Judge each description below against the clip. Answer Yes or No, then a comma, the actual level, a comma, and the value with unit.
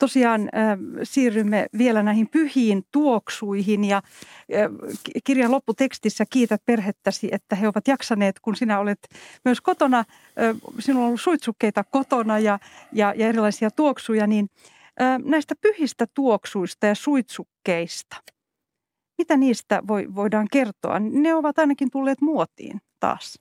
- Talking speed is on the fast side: No, average, 130 wpm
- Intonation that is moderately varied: Yes, average, 4.3 semitones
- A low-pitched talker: No, high, 230 Hz